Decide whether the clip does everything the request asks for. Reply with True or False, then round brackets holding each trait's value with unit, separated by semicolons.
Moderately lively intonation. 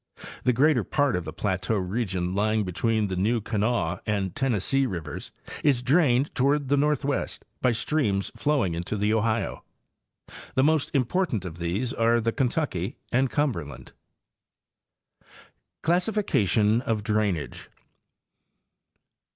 False (5.7 semitones)